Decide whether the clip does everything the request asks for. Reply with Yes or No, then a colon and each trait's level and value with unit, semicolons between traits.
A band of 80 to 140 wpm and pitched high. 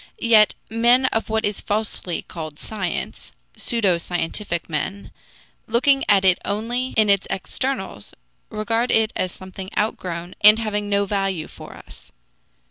Yes: slow, 135 wpm; high, 205 Hz